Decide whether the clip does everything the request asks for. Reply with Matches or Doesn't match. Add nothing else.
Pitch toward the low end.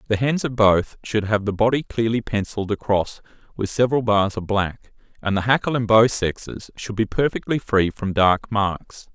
Matches